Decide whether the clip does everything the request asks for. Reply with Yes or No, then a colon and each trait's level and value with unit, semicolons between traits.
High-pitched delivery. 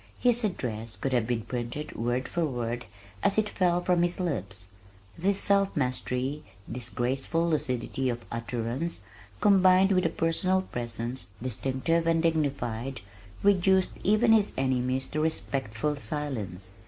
No: low, 135 Hz